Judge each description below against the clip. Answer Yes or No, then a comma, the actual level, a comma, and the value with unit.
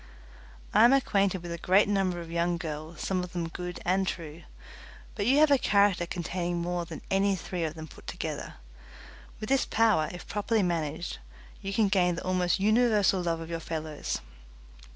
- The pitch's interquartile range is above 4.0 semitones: No, average, 3.0 semitones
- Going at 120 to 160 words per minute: No, average, 185 wpm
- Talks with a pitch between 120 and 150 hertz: No, medium, 180 Hz